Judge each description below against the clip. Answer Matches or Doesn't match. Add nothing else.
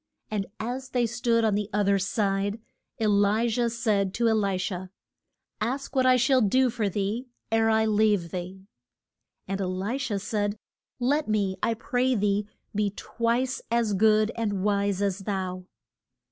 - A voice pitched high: Matches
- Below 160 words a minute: Doesn't match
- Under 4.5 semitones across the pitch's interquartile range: Matches